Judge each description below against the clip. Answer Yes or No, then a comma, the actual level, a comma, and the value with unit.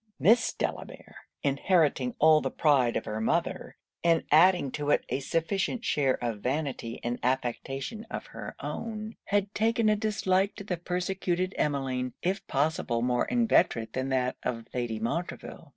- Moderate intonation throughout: No, wide, 7.2 semitones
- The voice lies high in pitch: No, medium, 155 Hz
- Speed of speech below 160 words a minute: Yes, average, 150 wpm